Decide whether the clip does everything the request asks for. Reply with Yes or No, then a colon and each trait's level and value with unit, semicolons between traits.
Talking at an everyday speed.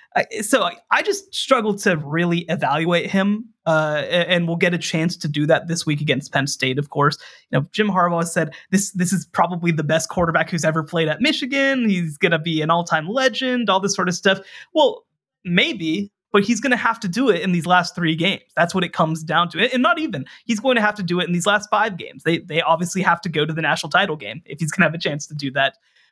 No: fast, 255 wpm